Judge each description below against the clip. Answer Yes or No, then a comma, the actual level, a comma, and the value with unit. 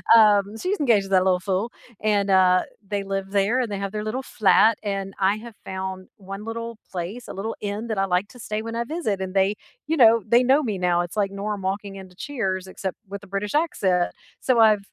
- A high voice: Yes, high, 200 Hz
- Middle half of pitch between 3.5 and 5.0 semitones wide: No, average, 2.8 semitones